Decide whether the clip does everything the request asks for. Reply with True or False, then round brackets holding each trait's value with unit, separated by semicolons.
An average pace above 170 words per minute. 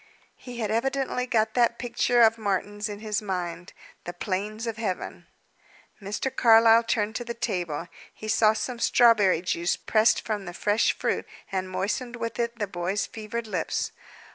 False (165 wpm)